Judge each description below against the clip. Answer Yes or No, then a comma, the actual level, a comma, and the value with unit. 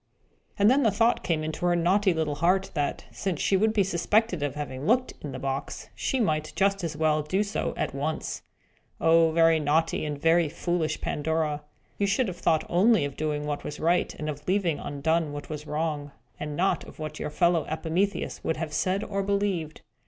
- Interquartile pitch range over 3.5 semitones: Yes, average, 4.2 semitones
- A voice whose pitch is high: No, medium, 165 Hz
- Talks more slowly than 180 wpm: No, average, 200 wpm